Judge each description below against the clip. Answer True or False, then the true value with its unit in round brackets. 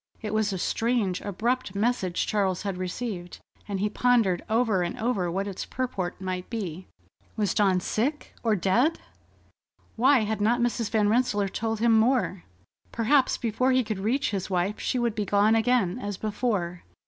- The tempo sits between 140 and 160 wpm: False (170 wpm)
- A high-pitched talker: True (215 Hz)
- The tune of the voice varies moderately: True (3.9 semitones)